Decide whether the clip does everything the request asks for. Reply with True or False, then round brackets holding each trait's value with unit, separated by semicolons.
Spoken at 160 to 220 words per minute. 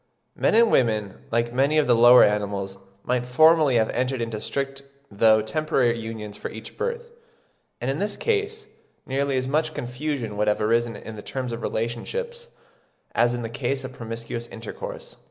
True (175 wpm)